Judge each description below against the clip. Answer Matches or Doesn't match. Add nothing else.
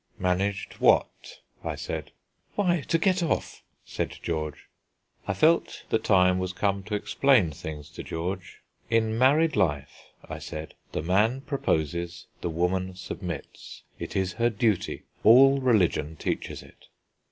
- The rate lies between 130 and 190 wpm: Matches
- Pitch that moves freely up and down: Matches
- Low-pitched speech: Matches